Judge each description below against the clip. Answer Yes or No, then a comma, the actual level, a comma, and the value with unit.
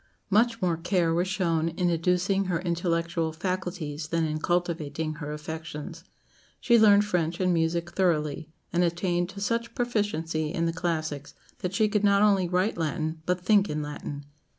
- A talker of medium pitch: Yes, medium, 170 Hz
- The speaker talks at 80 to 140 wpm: No, average, 165 wpm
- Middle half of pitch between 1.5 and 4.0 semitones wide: Yes, average, 2.9 semitones